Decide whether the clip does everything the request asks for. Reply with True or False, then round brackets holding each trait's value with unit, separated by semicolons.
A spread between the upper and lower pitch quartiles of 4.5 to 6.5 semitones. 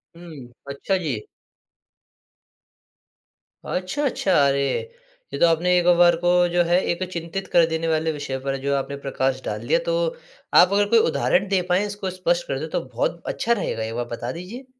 True (4.9 semitones)